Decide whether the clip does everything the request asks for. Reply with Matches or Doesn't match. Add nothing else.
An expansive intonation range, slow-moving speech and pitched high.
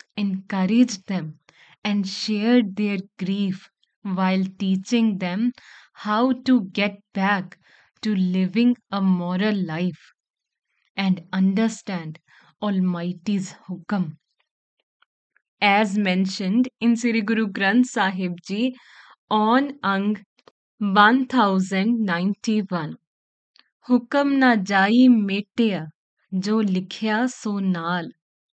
Doesn't match